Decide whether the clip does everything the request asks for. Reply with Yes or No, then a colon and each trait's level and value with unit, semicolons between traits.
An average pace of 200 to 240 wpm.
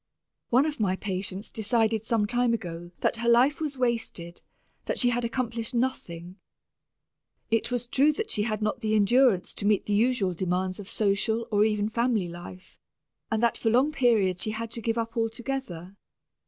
No: average, 180 wpm